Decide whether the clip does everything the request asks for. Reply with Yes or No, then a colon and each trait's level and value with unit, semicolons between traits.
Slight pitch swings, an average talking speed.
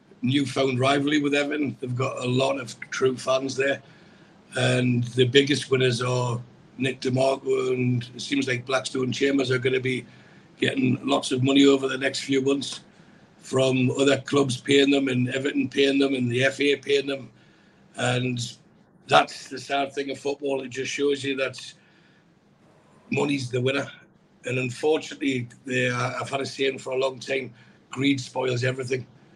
Yes: narrow, 1.4 semitones; average, 165 wpm